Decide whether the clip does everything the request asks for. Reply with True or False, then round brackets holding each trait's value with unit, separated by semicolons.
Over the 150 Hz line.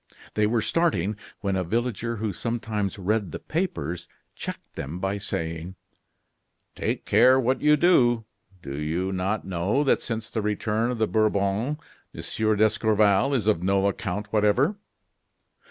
False (105 Hz)